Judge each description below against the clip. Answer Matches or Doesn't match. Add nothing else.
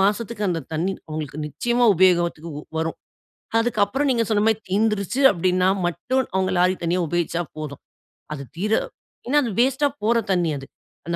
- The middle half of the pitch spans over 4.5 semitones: Matches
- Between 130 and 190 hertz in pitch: Matches